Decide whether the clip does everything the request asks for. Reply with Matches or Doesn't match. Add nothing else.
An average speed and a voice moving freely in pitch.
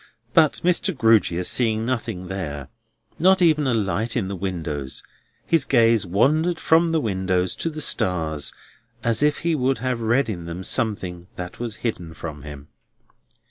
Matches